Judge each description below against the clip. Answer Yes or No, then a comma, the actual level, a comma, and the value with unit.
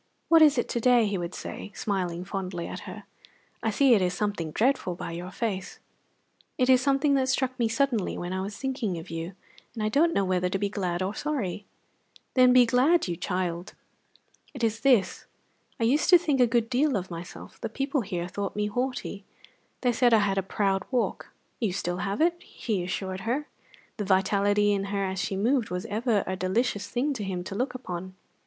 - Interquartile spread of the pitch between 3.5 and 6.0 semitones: Yes, average, 5.2 semitones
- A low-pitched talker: No, high, 210 Hz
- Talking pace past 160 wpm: Yes, fast, 205 wpm